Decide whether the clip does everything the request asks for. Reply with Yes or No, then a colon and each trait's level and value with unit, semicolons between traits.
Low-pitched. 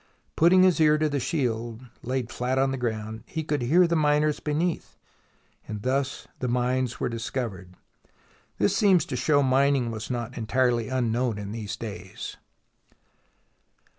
Yes: low, 130 Hz